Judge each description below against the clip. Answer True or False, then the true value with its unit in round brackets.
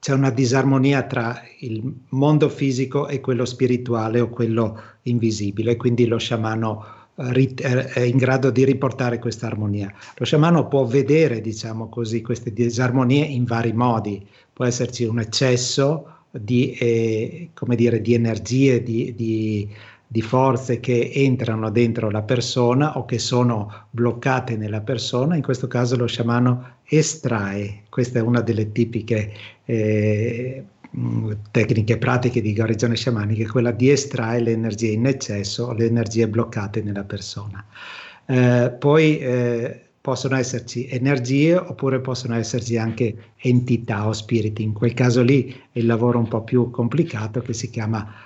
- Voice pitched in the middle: False (120 Hz)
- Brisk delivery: False (145 wpm)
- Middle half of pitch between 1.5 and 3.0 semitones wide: True (2.4 semitones)